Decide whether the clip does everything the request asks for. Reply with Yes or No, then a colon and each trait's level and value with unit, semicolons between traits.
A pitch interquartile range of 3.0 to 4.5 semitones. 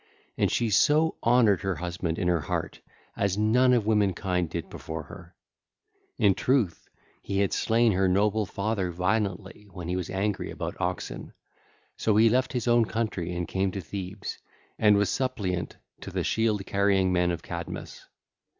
Yes: average, 3.4 semitones